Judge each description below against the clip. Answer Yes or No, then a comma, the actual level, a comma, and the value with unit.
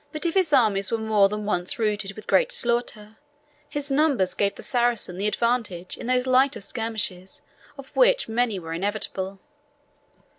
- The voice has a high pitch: Yes, high, 220 Hz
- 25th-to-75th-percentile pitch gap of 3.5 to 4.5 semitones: Yes, average, 4.2 semitones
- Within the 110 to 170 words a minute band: Yes, average, 160 wpm